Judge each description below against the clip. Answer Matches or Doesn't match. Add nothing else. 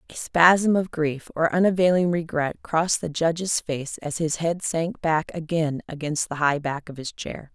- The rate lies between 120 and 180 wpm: Doesn't match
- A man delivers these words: Doesn't match